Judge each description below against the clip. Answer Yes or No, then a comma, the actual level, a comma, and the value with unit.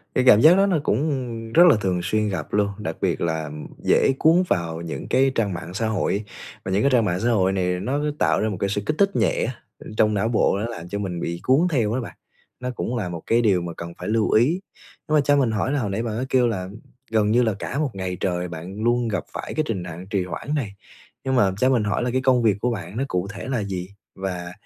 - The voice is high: No, low, 105 Hz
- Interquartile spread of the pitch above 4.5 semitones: Yes, average, 5.3 semitones